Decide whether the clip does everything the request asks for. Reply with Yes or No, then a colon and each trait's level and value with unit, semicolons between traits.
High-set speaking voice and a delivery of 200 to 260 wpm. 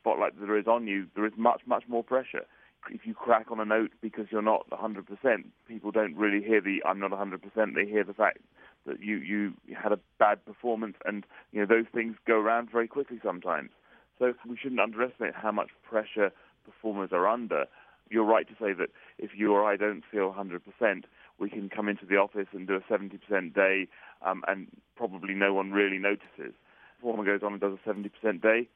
No: low, 105 Hz; fast, 205 wpm